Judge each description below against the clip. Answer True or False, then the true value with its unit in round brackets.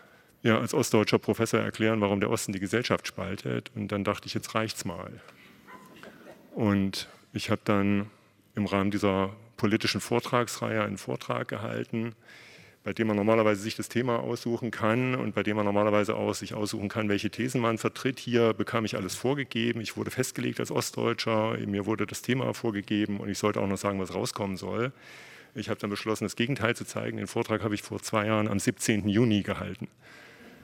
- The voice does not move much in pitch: True (2.1 semitones)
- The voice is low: True (105 Hz)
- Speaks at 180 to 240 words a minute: True (190 wpm)